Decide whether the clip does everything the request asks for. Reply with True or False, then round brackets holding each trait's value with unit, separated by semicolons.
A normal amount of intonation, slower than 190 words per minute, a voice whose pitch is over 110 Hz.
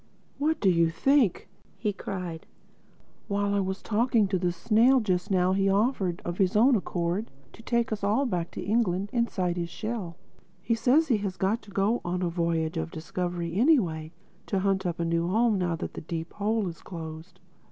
False (4.2 semitones; 195 wpm; 190 Hz)